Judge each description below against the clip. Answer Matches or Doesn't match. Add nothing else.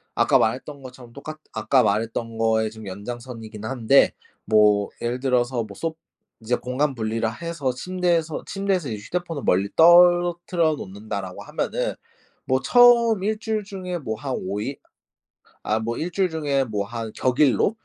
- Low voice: Matches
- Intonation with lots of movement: Matches